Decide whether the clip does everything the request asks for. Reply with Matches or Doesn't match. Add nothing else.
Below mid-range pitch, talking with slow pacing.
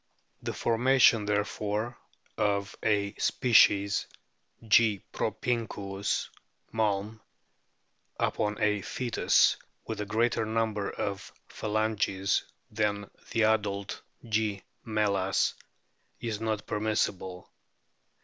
Matches